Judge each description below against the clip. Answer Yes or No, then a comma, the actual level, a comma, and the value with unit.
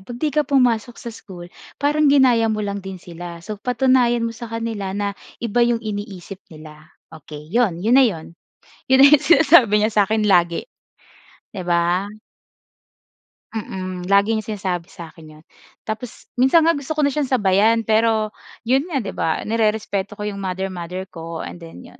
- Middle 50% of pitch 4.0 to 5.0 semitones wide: Yes, average, 4.6 semitones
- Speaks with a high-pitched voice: Yes, high, 215 Hz